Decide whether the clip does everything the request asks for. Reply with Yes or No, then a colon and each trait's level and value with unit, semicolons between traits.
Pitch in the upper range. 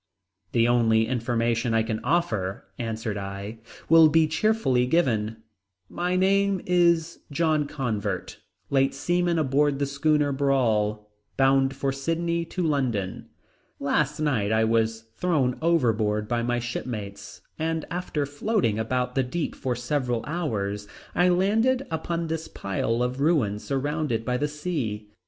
No: low, 135 Hz